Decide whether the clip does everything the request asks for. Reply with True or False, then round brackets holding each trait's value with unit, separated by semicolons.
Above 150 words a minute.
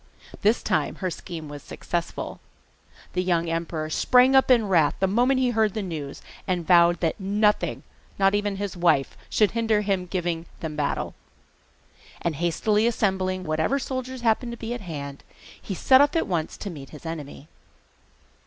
True (170 wpm)